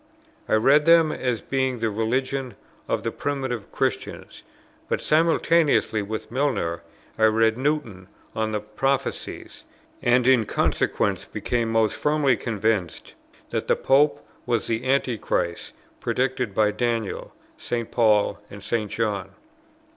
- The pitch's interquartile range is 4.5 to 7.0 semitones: No, average, 3.7 semitones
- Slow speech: Yes, slow, 125 wpm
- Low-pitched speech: Yes, low, 120 Hz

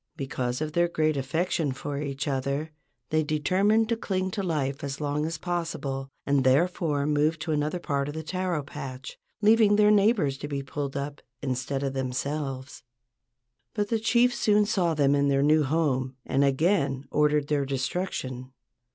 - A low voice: No, medium, 150 Hz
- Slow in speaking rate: No, average, 170 wpm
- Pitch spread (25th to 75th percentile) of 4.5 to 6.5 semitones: No, average, 4.1 semitones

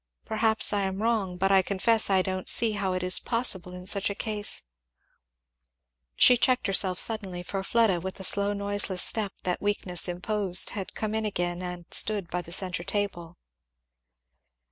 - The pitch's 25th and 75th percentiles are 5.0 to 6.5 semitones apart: No, narrow, 2.6 semitones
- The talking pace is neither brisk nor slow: Yes, average, 170 wpm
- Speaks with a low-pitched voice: No, high, 195 Hz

